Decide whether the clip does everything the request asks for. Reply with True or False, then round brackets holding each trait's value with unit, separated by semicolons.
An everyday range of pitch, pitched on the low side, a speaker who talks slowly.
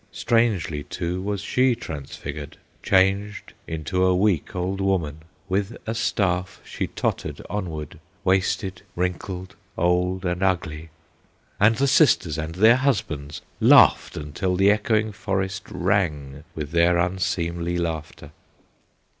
True (3.3 semitones; 90 Hz; 120 wpm)